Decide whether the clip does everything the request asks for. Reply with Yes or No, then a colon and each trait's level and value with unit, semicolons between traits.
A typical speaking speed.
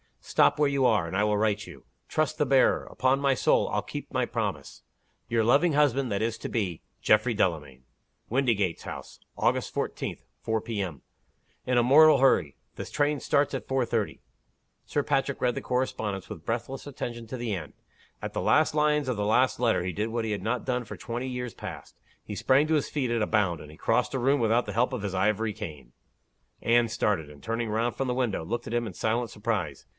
No: fast, 215 wpm